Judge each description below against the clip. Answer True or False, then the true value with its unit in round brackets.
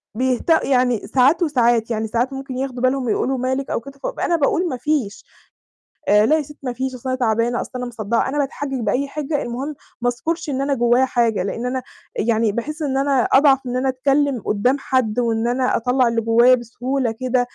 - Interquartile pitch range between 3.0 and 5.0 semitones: False (2.4 semitones)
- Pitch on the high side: True (255 Hz)